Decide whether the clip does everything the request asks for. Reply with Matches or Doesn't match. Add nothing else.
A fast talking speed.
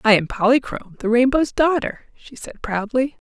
Doesn't match